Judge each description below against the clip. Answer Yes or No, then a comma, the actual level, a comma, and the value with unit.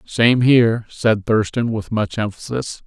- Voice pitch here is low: Yes, low, 115 Hz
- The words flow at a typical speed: Yes, average, 145 wpm